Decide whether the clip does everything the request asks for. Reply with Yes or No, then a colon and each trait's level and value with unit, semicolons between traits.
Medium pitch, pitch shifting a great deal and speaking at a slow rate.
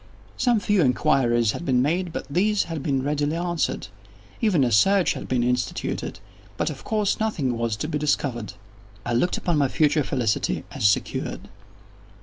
No: medium, 145 Hz; wide, 6.1 semitones; average, 160 wpm